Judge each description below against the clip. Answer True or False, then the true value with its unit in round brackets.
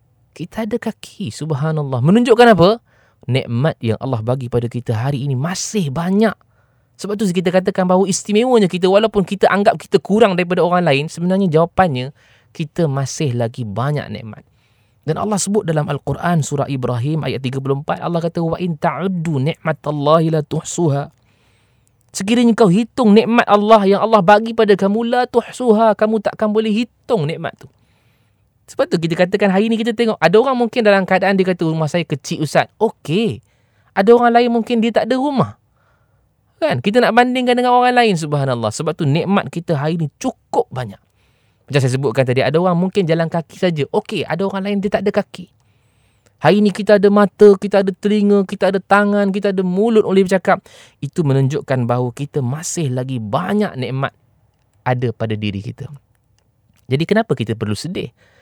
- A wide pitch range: True (8.2 semitones)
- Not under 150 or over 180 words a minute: True (175 wpm)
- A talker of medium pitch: True (165 Hz)